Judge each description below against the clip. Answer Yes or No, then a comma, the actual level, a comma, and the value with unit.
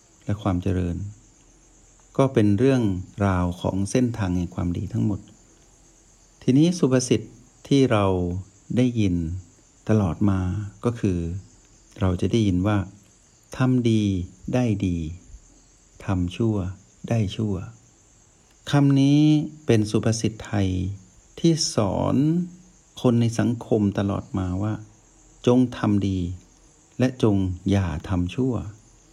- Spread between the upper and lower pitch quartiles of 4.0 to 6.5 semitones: Yes, average, 4.4 semitones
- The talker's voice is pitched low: Yes, low, 105 Hz